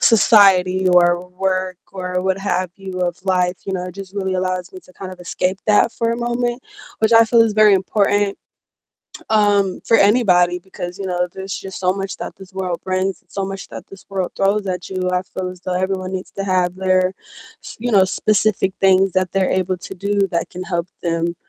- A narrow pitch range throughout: Yes, narrow, 1.5 semitones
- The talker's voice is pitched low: No, high, 190 Hz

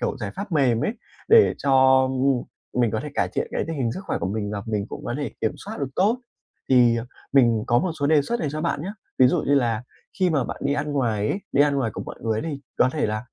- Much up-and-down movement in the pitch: No, average, 4.5 semitones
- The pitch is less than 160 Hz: Yes, low, 135 Hz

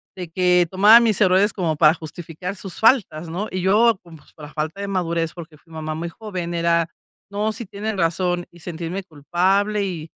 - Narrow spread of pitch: No, average, 3.3 semitones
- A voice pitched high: No, medium, 180 Hz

